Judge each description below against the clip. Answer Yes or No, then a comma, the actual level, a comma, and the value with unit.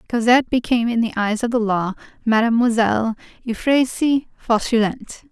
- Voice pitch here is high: Yes, high, 235 Hz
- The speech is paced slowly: Yes, slow, 125 wpm